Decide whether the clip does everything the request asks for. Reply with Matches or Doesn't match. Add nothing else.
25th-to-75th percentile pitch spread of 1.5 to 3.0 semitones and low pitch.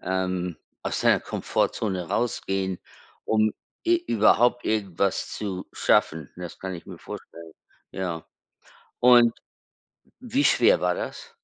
Doesn't match